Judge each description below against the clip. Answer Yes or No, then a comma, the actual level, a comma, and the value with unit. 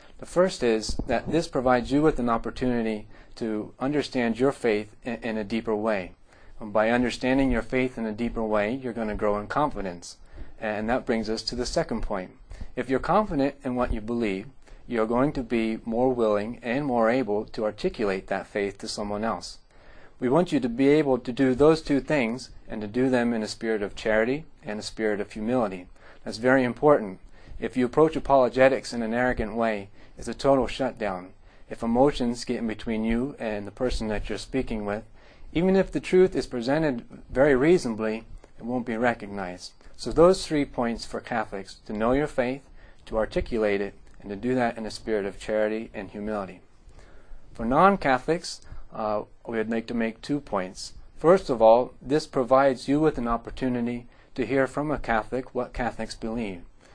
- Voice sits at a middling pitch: No, low, 115 Hz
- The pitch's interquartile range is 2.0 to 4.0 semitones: Yes, average, 3.3 semitones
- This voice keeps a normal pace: Yes, average, 190 wpm